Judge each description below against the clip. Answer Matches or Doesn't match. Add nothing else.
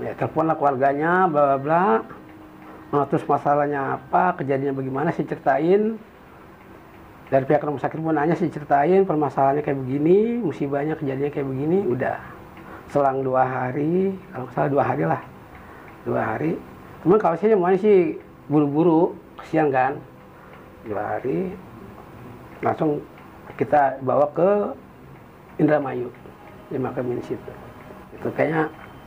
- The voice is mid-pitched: Matches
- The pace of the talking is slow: Doesn't match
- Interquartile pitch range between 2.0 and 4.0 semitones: Matches